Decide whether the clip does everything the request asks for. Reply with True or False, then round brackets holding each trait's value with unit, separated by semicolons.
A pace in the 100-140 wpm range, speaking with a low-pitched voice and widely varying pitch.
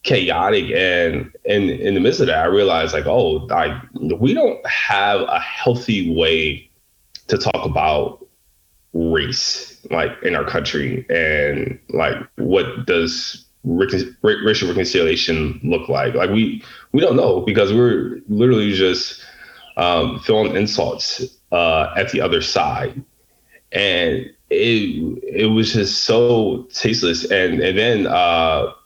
True (135 wpm; 105 Hz; 6.9 semitones)